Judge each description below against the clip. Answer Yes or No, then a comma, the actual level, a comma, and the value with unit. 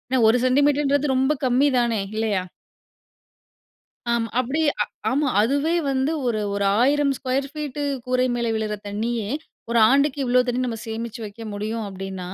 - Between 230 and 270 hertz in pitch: Yes, very high, 250 Hz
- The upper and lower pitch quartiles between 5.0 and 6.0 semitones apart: No, average, 4.0 semitones